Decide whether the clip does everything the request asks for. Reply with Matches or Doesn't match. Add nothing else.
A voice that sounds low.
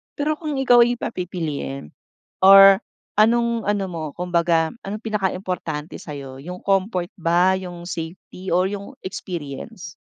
Doesn't match